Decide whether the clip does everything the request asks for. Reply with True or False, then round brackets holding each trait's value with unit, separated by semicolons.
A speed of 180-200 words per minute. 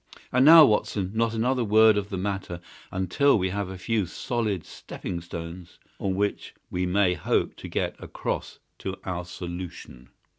False (160 wpm)